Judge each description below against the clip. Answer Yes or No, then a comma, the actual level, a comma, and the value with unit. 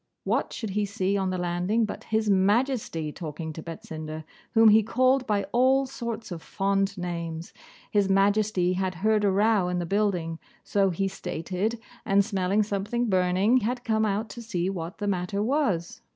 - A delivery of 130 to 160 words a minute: No, average, 175 wpm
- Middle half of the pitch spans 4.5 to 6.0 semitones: No, average, 3.5 semitones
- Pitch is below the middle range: No, high, 200 Hz